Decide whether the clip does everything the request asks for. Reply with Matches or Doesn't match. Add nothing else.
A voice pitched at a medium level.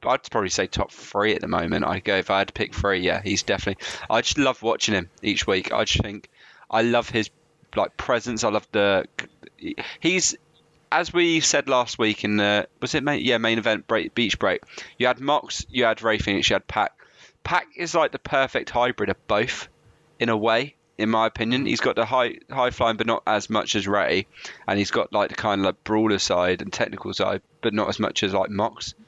Doesn't match